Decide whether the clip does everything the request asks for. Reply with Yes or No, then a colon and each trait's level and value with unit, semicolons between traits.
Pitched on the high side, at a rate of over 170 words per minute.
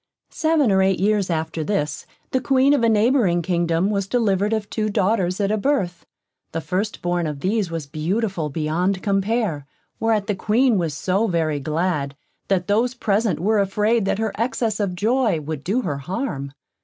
Yes: high, 195 Hz; average, 180 wpm